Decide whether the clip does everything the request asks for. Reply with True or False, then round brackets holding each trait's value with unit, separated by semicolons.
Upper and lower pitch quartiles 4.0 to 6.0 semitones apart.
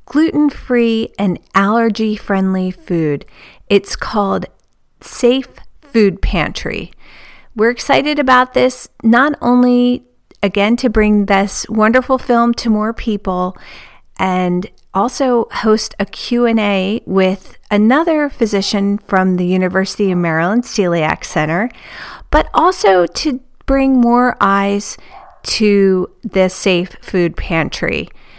True (4.4 semitones)